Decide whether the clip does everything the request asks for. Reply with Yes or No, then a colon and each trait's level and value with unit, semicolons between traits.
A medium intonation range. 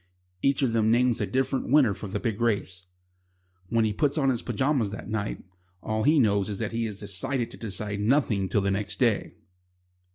Yes: average, 4.1 semitones